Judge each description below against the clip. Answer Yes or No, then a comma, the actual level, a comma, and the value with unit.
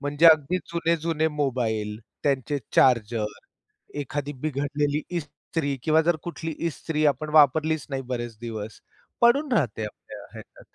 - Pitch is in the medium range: Yes, medium, 145 Hz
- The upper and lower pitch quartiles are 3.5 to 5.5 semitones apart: Yes, average, 4.0 semitones